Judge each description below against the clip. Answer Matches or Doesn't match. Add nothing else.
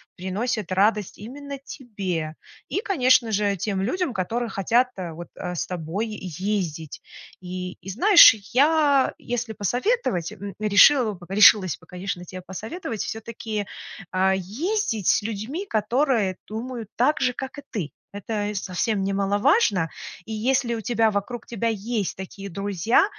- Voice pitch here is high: Matches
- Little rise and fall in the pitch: Doesn't match